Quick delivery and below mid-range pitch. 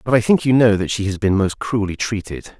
Yes: fast, 275 wpm; low, 105 Hz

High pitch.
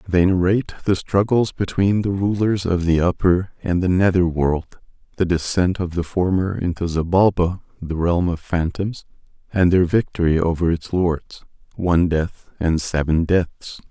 No: very low, 90 Hz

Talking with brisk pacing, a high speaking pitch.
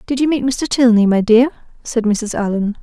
Yes: fast, 210 wpm; high, 235 Hz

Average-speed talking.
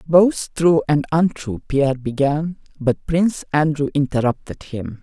No: slow, 130 wpm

